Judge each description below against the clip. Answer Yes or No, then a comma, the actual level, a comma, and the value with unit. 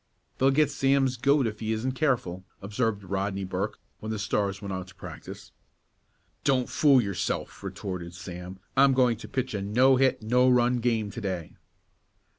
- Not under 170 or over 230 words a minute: Yes, average, 175 wpm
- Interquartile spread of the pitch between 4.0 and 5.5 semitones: Yes, average, 4.9 semitones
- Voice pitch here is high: No, low, 110 Hz